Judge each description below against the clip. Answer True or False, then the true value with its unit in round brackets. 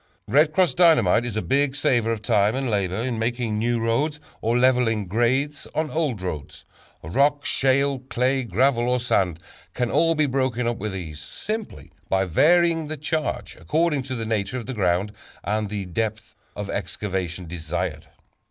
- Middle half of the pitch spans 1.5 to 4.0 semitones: False (5.5 semitones)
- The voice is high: False (120 Hz)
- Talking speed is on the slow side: False (170 wpm)